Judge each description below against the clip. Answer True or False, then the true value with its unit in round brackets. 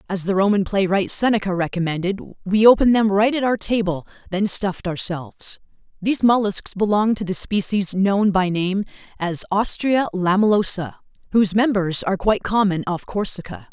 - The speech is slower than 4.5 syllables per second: False (5.4 syllables/s)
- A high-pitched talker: True (200 Hz)